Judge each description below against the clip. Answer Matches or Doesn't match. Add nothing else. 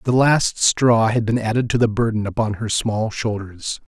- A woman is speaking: Doesn't match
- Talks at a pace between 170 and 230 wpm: Matches